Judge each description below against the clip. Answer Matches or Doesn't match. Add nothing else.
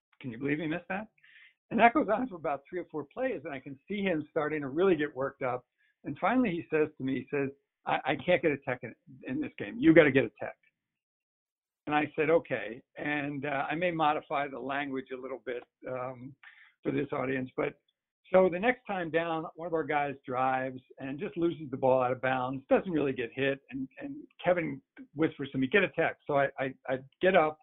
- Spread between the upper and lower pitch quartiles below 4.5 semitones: Doesn't match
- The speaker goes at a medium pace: Doesn't match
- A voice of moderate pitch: Matches